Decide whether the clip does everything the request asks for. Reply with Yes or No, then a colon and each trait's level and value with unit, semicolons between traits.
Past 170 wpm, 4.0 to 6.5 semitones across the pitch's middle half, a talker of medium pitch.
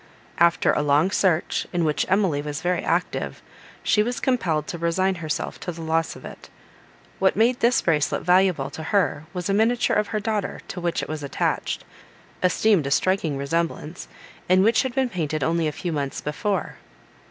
Yes: average, 185 wpm; average, 4.4 semitones; medium, 175 Hz